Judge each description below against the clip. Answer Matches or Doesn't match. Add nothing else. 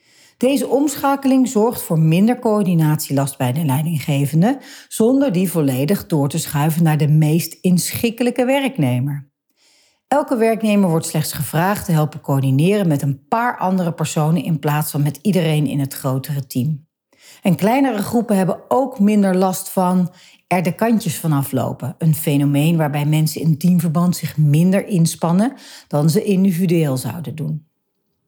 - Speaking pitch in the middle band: Matches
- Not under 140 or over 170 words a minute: Matches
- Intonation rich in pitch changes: Matches